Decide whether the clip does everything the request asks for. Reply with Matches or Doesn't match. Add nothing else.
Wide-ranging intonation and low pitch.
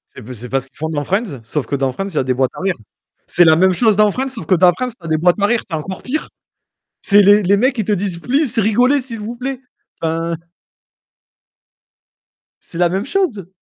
Doesn't match